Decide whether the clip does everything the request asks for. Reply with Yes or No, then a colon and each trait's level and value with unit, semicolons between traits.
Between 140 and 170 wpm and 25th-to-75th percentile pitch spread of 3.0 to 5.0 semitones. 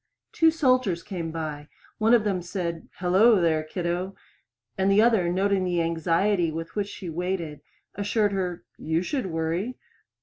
Yes: average, 155 wpm; average, 3.5 semitones